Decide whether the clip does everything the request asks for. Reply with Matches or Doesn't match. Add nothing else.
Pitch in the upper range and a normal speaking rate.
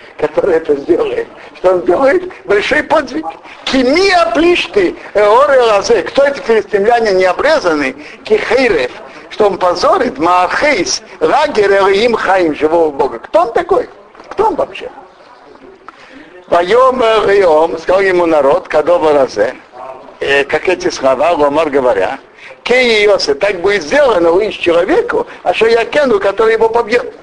Matches